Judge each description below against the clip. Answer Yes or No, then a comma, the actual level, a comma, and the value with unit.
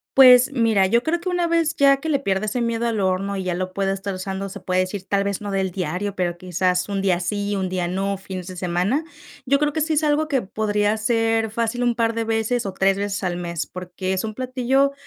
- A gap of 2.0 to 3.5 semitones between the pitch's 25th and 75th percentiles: No, average, 4.5 semitones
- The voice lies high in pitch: Yes, high, 200 Hz